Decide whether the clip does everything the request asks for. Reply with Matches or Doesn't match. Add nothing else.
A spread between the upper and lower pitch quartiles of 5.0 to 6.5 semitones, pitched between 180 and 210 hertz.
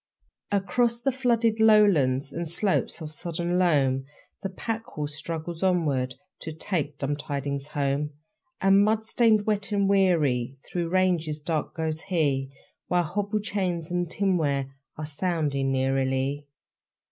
Doesn't match